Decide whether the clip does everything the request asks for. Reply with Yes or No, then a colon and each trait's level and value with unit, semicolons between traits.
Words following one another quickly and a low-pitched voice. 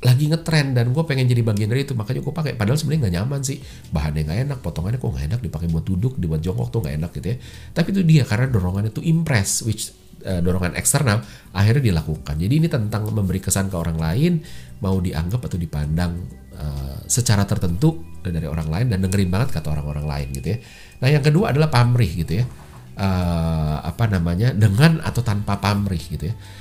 Yes: fast, 200 wpm; low, 100 Hz